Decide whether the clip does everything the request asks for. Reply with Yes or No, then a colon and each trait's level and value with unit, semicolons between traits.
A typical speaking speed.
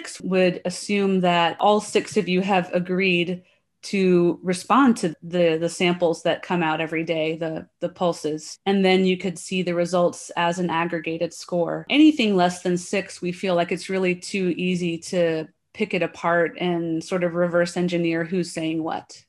Yes: average, 175 wpm